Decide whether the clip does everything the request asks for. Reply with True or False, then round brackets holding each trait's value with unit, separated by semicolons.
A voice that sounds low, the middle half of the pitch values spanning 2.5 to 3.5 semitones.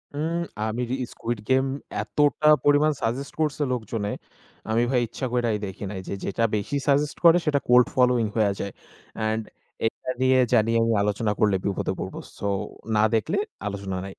False (115 Hz; 4.3 semitones)